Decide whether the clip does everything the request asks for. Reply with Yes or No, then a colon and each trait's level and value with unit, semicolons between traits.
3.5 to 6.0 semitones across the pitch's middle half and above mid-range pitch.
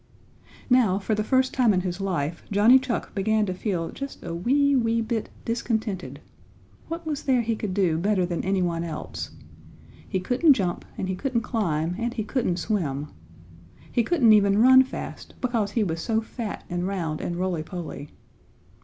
Yes: average, 5.1 semitones; high, 210 Hz